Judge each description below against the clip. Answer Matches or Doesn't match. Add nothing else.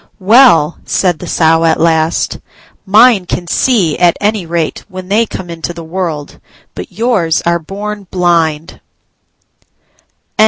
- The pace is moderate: Doesn't match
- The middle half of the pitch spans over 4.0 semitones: Doesn't match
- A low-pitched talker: Doesn't match